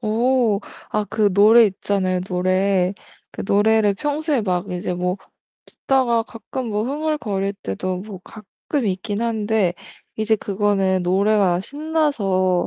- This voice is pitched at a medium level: No, high, 205 Hz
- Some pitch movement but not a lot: Yes, average, 3.4 semitones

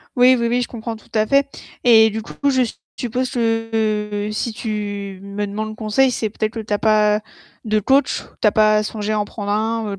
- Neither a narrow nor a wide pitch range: No, narrow, 1.7 semitones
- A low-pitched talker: No, high, 215 Hz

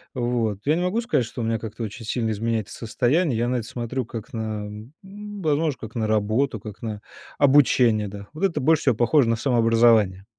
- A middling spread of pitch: Yes, average, 4.2 semitones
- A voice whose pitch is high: No, low, 115 Hz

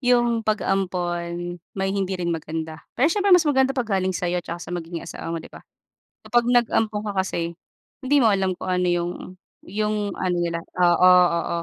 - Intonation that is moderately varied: Yes, average, 4.3 semitones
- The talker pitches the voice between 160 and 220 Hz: Yes, medium, 185 Hz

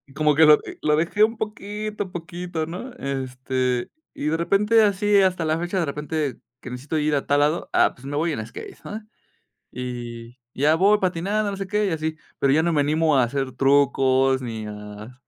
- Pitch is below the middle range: No, medium, 155 Hz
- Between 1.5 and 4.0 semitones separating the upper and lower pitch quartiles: No, wide, 5.6 semitones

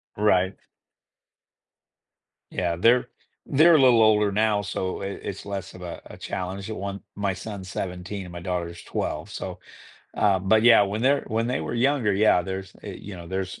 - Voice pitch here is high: No, low, 100 Hz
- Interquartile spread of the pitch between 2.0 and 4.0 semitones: Yes, average, 2.9 semitones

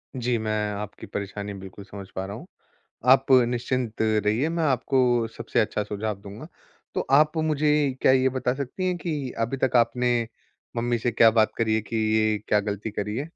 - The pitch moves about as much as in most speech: Yes, average, 3.9 semitones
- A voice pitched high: No, low, 115 Hz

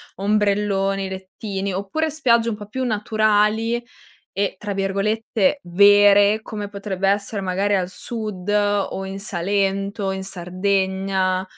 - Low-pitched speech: No, high, 200 Hz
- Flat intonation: Yes, narrow, 1.6 semitones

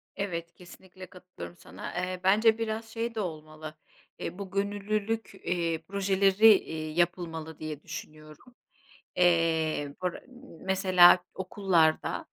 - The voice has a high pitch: No, medium, 180 Hz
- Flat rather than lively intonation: No, average, 3.6 semitones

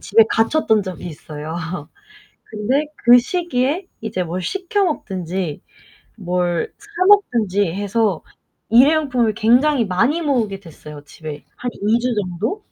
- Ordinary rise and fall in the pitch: No, wide, 6.7 semitones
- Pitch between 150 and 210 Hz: No, high, 220 Hz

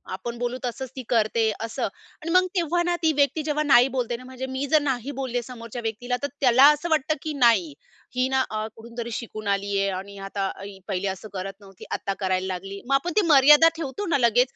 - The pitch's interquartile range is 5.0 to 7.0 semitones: Yes, average, 5.3 semitones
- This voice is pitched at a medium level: No, high, 245 Hz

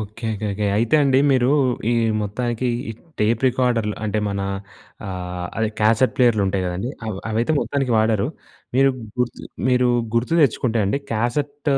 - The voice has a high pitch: No, low, 115 Hz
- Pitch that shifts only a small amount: No, average, 3.1 semitones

